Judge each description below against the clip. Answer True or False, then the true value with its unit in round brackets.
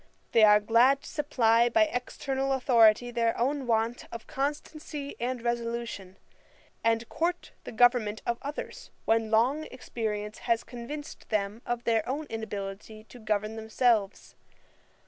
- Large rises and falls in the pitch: False (3.1 semitones)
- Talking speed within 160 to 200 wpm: False (135 wpm)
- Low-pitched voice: False (235 Hz)